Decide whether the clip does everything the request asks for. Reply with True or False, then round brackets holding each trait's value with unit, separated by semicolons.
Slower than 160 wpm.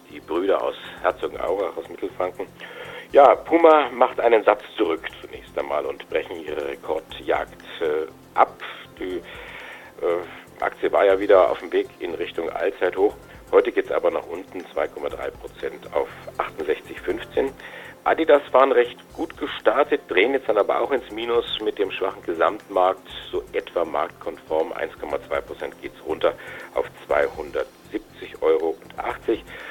True (135 wpm)